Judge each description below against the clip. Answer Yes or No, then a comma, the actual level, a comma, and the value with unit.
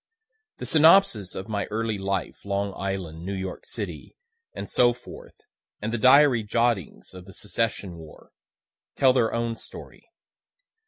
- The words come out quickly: No, average, 145 wpm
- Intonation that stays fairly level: No, average, 3.5 semitones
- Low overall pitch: Yes, low, 105 Hz